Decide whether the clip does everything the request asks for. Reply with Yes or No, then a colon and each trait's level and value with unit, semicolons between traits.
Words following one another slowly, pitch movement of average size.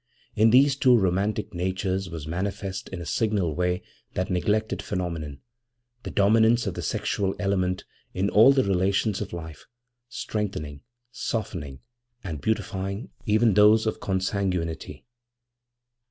Yes: slow, 125 wpm; average, 3.2 semitones